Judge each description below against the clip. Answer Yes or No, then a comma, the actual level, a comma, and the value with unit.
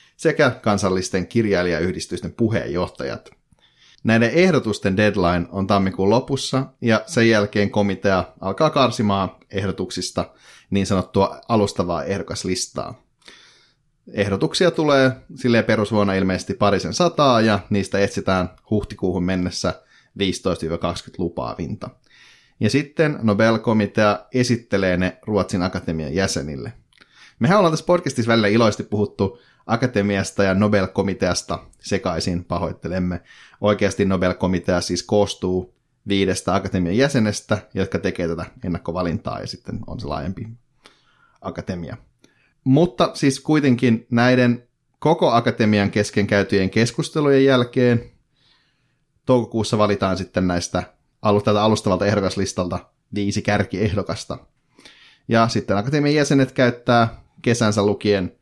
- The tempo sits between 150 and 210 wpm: No, average, 100 wpm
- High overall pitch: No, low, 105 Hz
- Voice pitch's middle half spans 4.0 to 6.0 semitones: Yes, average, 4.4 semitones